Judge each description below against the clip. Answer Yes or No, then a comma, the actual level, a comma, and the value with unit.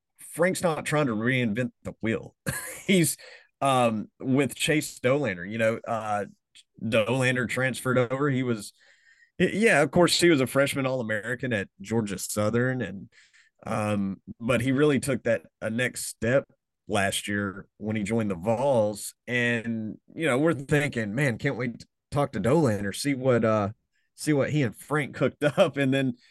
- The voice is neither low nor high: No, low, 125 Hz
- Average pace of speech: Yes, average, 165 wpm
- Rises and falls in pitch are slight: No, average, 4.5 semitones